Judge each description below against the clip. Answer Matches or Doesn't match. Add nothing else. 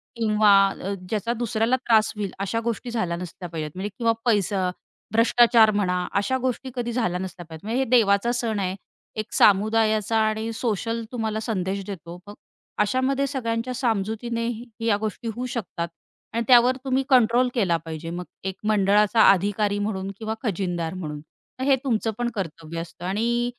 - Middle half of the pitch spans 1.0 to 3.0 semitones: Doesn't match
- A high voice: Matches